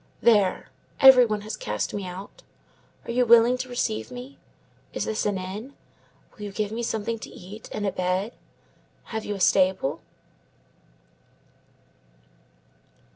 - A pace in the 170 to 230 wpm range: No, average, 140 wpm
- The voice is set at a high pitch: Yes, high, 215 Hz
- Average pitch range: Yes, average, 3.5 semitones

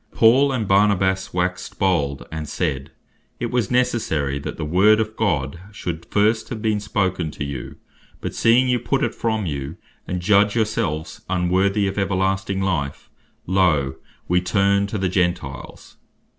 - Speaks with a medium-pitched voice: No, very low, 95 Hz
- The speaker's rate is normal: Yes, average, 160 wpm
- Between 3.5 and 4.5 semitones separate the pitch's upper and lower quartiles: Yes, average, 4.2 semitones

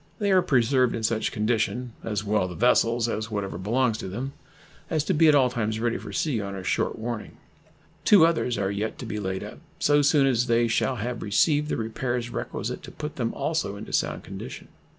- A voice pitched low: Yes, low, 120 Hz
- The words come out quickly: Yes, fast, 210 wpm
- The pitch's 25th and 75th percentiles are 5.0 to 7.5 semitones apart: No, average, 3.9 semitones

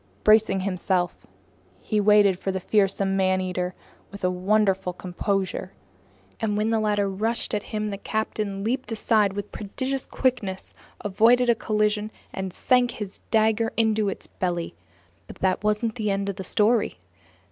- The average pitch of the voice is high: Yes, high, 210 Hz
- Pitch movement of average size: No, narrow, 2.3 semitones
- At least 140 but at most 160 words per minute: Yes, average, 150 wpm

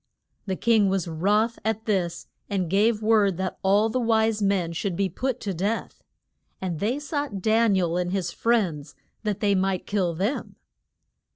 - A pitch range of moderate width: Yes, average, 3.2 semitones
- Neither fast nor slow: Yes, average, 175 wpm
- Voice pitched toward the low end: No, high, 200 Hz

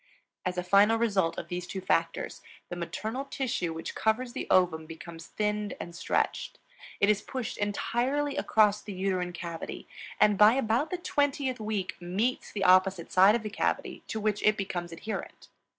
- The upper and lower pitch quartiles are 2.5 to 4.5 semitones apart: Yes, average, 4.0 semitones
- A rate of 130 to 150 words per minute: No, average, 170 wpm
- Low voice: No, high, 205 Hz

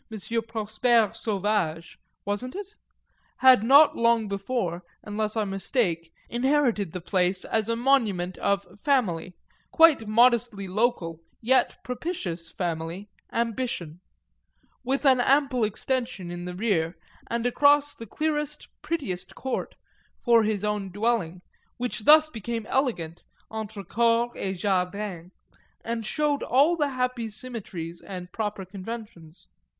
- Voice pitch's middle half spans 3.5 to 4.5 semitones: No, average, 5.2 semitones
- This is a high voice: Yes, high, 220 Hz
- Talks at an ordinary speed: No, slow, 120 wpm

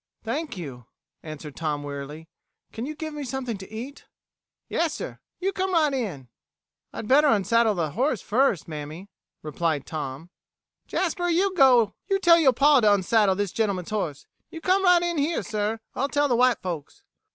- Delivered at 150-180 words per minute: Yes, average, 165 wpm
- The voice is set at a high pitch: Yes, high, 225 Hz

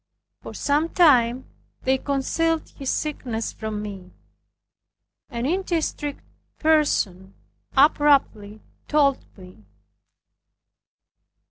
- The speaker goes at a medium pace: No, slow, 80 wpm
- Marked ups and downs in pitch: Yes, wide, 5.7 semitones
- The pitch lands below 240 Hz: No, very high, 270 Hz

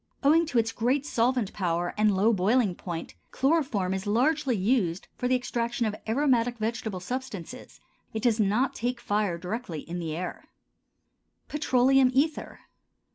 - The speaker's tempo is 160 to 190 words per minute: No, average, 145 wpm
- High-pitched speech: Yes, high, 230 Hz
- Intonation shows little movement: No, average, 5.0 semitones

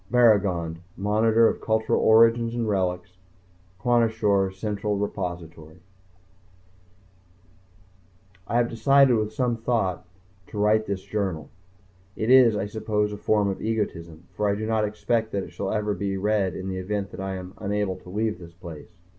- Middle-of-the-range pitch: No, low, 105 Hz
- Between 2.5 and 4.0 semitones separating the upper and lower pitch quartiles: Yes, average, 2.8 semitones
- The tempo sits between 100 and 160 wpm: Yes, average, 155 wpm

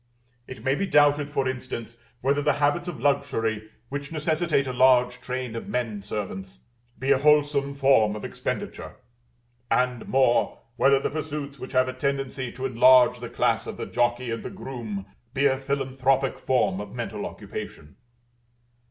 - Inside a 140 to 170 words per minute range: Yes, average, 160 wpm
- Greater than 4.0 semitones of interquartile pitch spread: No, average, 2.7 semitones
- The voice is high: No, low, 130 Hz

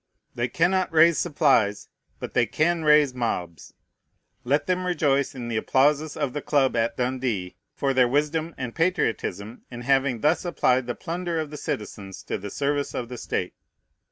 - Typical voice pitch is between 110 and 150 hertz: Yes, medium, 140 Hz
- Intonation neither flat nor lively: Yes, average, 4.6 semitones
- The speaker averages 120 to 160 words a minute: No, average, 170 wpm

